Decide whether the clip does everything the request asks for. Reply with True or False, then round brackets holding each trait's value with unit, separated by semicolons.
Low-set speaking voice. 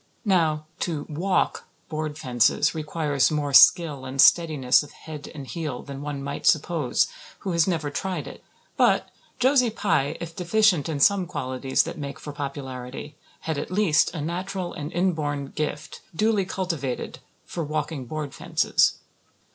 False (155 Hz)